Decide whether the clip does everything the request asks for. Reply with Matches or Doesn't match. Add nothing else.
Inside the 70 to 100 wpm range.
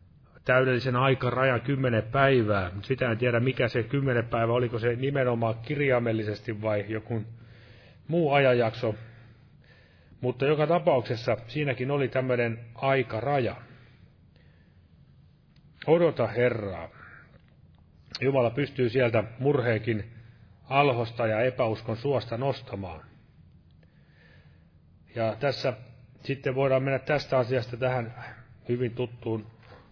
Matches